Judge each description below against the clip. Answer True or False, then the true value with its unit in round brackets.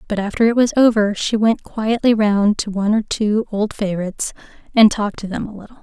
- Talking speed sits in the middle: False (215 wpm)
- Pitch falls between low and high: False (210 Hz)